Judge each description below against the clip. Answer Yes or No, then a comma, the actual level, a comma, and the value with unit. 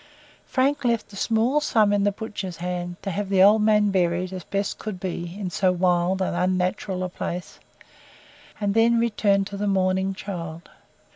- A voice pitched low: No, high, 195 Hz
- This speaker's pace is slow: No, average, 175 wpm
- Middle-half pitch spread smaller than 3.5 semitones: Yes, narrow, 2.6 semitones